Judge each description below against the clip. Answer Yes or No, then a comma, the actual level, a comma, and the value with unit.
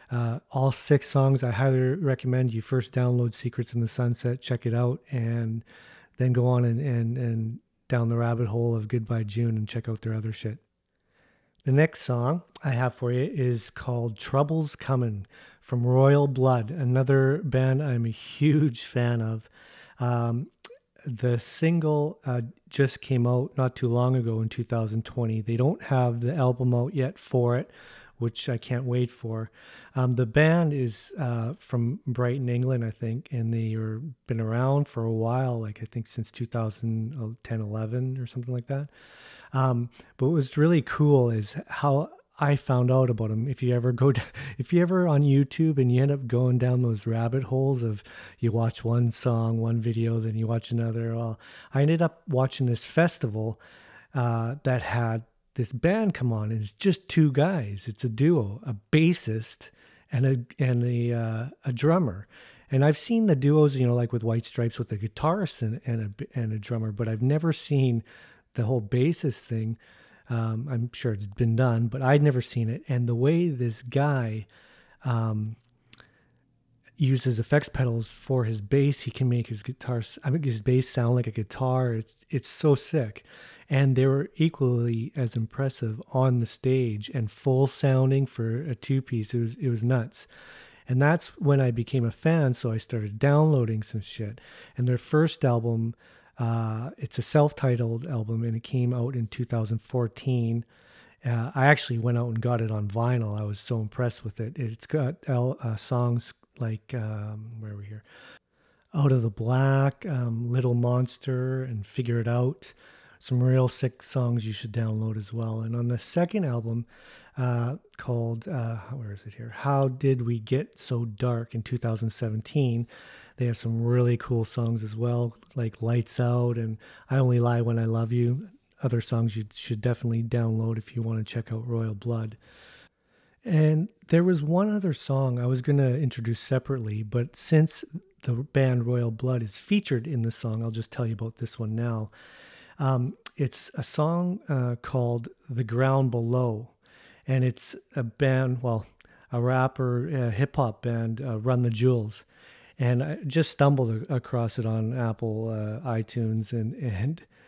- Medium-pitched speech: No, low, 125 Hz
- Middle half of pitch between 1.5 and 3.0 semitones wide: Yes, narrow, 2.6 semitones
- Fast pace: No, average, 180 wpm